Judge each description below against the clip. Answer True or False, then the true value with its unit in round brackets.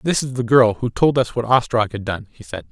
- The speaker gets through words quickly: True (285 wpm)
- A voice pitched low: True (120 Hz)